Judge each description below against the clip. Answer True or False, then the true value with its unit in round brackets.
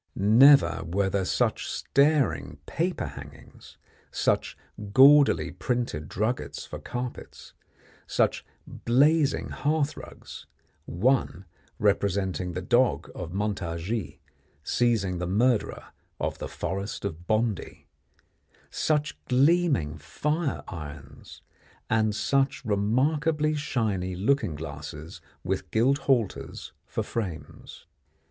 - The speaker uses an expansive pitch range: True (7.2 semitones)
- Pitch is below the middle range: True (110 Hz)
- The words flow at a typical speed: False (95 wpm)